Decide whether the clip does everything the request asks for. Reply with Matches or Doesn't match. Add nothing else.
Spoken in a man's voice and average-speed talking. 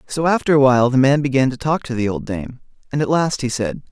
Doesn't match